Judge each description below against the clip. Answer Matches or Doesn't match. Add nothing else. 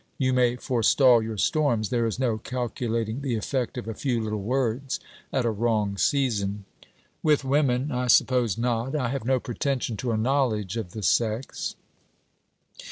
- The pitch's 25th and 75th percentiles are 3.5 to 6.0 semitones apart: Doesn't match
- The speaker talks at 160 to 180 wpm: Matches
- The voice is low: Matches